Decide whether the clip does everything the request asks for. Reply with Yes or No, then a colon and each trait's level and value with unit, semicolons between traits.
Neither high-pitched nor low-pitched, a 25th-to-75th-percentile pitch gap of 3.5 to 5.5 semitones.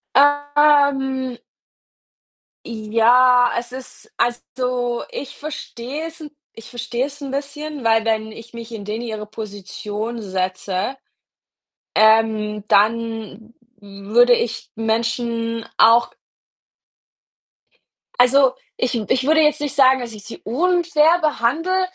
No: high, 240 Hz; average, 4.0 semitones